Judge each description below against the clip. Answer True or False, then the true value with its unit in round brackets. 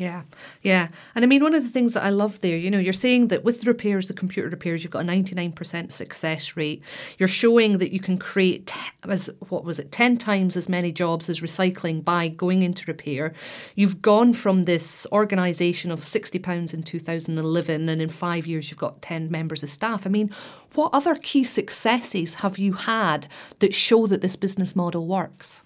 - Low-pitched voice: False (185 Hz)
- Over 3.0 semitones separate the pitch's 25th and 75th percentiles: True (3.5 semitones)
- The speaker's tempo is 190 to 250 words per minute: True (200 wpm)